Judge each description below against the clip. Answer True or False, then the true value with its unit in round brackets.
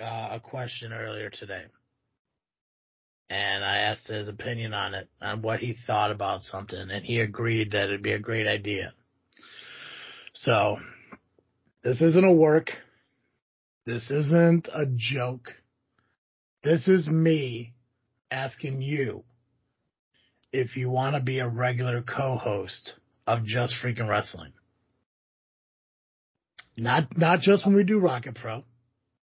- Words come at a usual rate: False (125 wpm)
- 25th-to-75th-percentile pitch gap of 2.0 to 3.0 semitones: False (3.5 semitones)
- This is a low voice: True (120 Hz)